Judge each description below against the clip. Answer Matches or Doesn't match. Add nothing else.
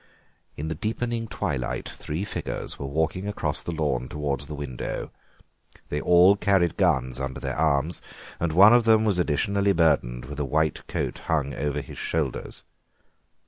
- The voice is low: Matches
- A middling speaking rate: Matches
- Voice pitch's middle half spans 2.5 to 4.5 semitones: Doesn't match